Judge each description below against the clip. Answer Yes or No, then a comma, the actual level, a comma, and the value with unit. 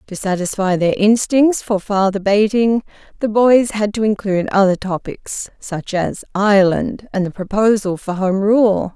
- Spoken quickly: No, average, 155 wpm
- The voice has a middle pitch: No, high, 205 Hz